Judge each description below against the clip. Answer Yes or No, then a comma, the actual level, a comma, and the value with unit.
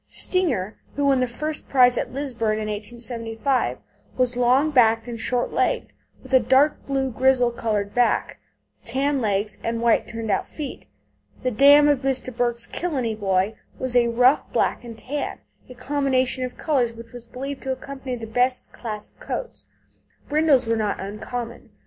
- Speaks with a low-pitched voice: No, high, 245 Hz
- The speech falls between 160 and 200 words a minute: Yes, average, 165 wpm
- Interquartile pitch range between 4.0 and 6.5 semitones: No, average, 2.8 semitones